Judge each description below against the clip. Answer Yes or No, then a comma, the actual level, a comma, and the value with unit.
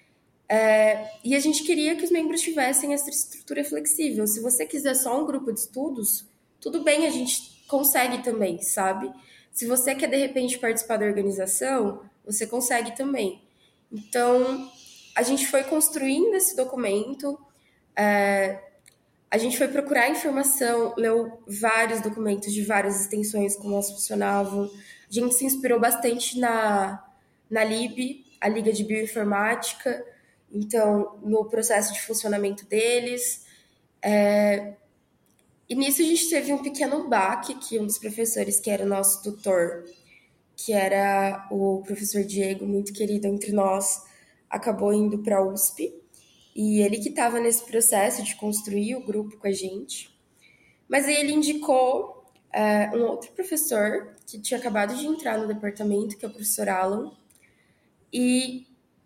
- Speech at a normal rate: Yes, average, 145 wpm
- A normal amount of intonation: Yes, average, 4.1 semitones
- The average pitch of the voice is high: Yes, high, 220 Hz